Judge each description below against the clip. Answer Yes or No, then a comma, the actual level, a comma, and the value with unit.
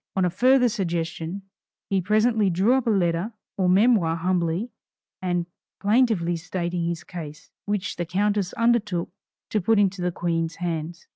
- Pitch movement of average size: Yes, average, 3.6 semitones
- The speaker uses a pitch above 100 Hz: Yes, medium, 185 Hz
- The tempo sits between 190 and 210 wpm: No, average, 150 wpm